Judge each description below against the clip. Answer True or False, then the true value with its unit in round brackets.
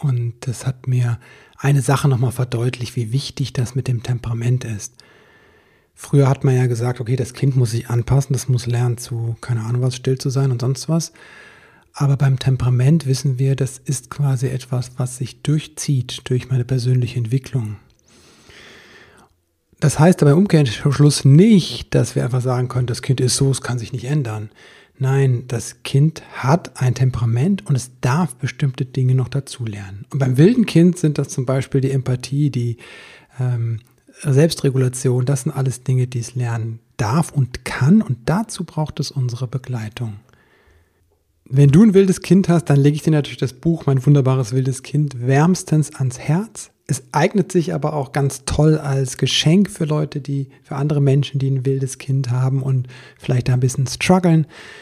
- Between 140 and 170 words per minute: False (180 wpm)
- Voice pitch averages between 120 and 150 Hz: True (135 Hz)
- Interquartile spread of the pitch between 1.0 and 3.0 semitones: True (2.7 semitones)